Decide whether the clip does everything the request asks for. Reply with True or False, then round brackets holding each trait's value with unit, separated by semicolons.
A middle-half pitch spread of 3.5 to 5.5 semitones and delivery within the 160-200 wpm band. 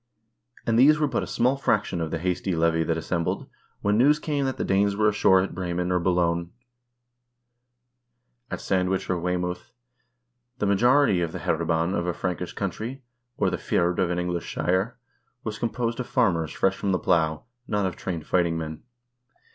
True (4.1 semitones; 180 wpm)